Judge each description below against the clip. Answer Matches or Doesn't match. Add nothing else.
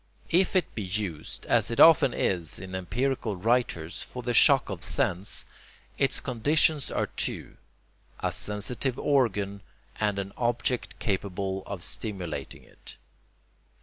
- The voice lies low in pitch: Matches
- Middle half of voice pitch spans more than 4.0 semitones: Matches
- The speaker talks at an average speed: Doesn't match